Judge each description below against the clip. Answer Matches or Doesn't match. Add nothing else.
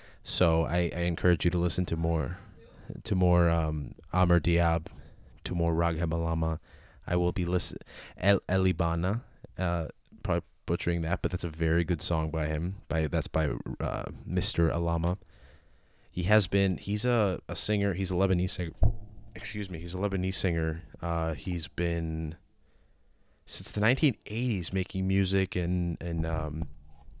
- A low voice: Matches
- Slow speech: Doesn't match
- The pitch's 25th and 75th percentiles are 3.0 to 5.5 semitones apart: Doesn't match